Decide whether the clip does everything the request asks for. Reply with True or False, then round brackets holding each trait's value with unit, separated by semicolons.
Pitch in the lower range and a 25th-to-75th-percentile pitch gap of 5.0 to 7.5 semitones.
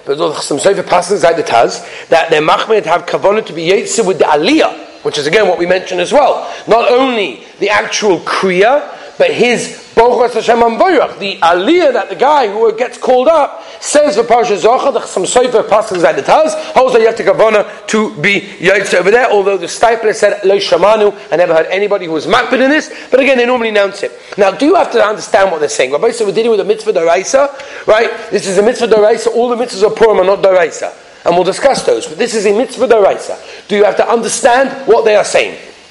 False (230 Hz; 5.6 semitones)